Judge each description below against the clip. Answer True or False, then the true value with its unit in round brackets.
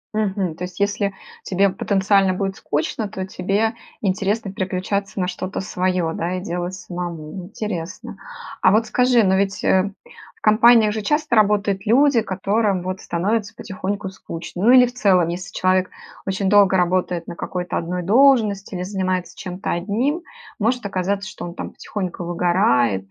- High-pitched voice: True (195 Hz)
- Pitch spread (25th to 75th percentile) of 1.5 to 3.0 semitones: True (2.6 semitones)